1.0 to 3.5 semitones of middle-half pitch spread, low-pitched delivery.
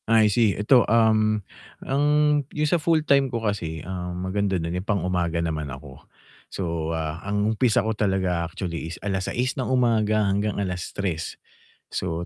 No: average, 4.3 semitones; low, 100 Hz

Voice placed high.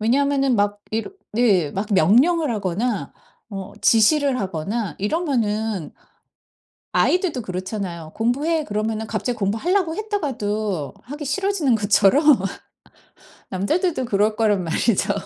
Yes: high, 220 Hz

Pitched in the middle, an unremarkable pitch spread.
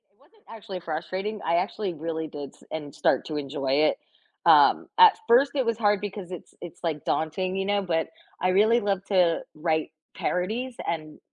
Yes: medium, 180 Hz; average, 4.6 semitones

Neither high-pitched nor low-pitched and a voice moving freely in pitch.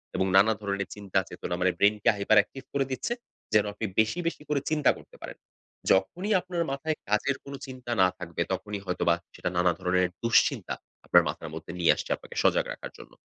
No: low, 105 Hz; wide, 6.5 semitones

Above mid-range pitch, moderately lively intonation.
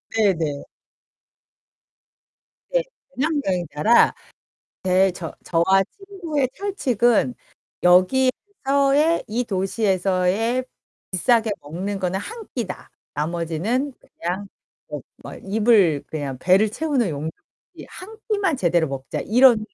No: high, 210 Hz; wide, 6.8 semitones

